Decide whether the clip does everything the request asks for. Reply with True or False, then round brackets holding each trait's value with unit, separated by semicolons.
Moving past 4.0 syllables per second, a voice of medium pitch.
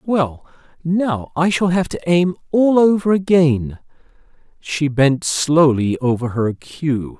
False (3.5 syllables/s; 155 Hz)